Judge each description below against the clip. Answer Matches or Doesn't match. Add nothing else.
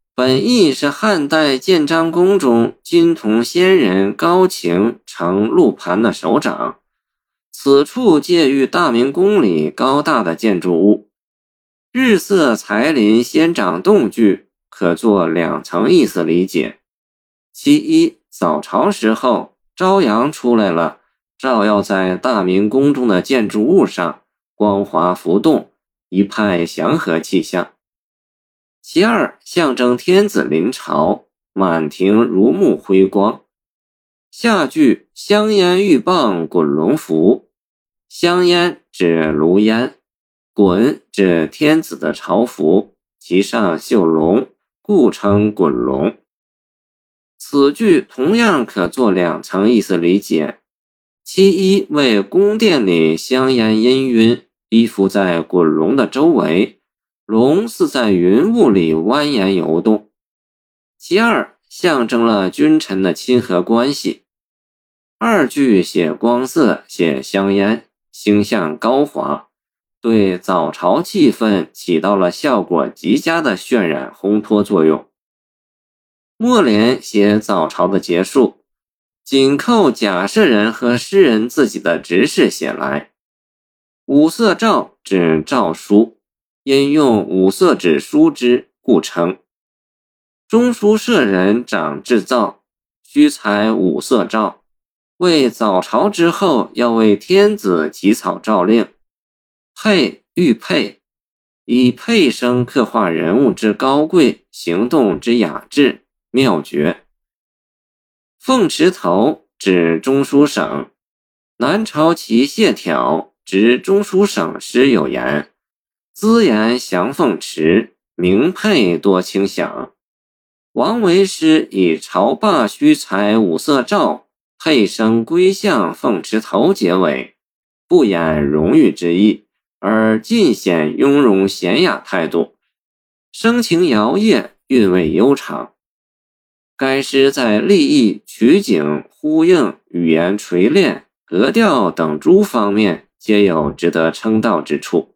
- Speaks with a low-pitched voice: Matches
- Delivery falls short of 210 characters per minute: Matches